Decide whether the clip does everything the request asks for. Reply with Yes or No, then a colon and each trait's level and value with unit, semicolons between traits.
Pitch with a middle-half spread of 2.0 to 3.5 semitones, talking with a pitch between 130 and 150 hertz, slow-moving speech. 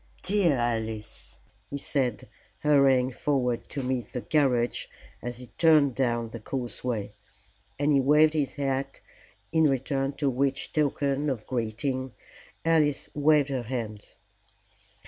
Yes: average, 3.1 semitones; low, 135 Hz; slow, 125 wpm